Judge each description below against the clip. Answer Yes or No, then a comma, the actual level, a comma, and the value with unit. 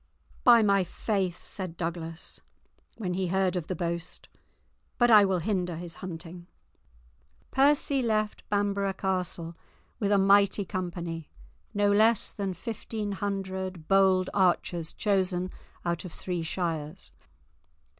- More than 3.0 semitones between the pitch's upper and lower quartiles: No, average, 2.7 semitones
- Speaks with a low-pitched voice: No, medium, 185 Hz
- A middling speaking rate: No, slow, 125 wpm